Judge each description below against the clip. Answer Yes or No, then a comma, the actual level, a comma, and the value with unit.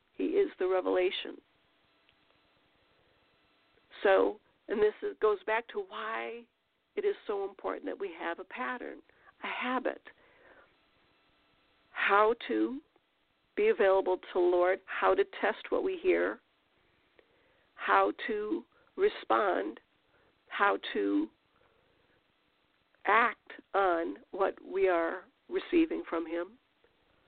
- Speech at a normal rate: No, slow, 105 wpm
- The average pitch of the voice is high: Yes, very high, 335 Hz